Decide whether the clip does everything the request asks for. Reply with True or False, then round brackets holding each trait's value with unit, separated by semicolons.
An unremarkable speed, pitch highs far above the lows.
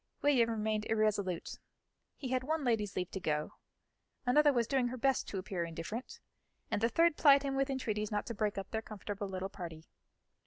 False (190 wpm; 4.8 semitones)